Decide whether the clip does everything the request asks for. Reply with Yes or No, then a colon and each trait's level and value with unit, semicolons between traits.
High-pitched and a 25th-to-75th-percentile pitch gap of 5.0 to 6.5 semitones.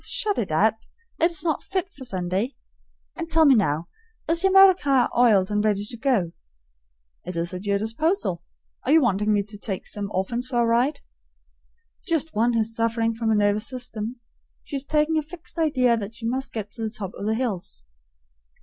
Yes: high, 230 Hz; wide, 5.5 semitones